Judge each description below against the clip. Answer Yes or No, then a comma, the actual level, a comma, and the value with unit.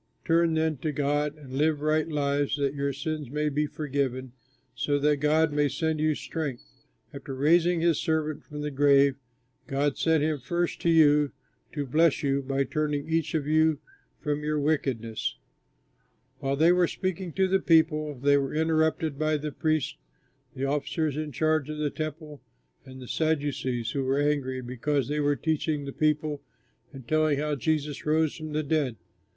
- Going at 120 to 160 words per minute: No, average, 175 wpm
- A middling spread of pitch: No, narrow, 1.9 semitones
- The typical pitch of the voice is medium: Yes, medium, 150 Hz